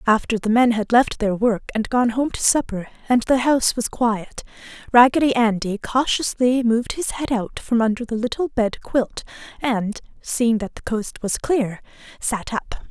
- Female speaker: Yes, female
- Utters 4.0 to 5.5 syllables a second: Yes, 4.6 syllables/s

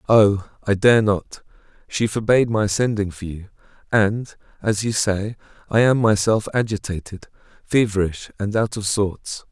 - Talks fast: No, average, 140 wpm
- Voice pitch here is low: Yes, low, 105 Hz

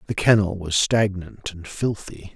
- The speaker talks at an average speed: Yes, average, 155 wpm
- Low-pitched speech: Yes, very low, 95 Hz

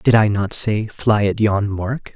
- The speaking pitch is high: No, low, 105 Hz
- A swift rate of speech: Yes, fast, 225 wpm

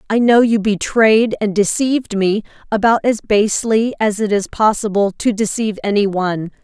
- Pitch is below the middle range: No, high, 215 Hz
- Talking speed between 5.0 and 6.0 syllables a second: Yes, 5.1 syllables/s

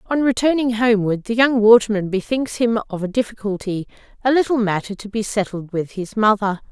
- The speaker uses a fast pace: No, average, 170 wpm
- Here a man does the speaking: No, female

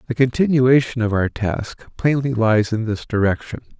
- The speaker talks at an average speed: Yes, average, 160 wpm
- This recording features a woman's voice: No, male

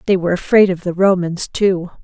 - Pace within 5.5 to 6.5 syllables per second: Yes, 5.7 syllables/s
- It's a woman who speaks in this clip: Yes, female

